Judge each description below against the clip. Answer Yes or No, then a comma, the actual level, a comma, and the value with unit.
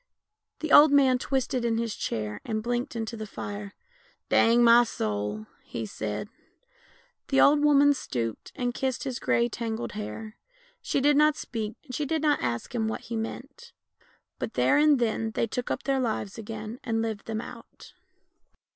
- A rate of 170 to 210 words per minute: Yes, average, 175 wpm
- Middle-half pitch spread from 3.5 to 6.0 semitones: Yes, average, 3.8 semitones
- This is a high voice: Yes, high, 235 Hz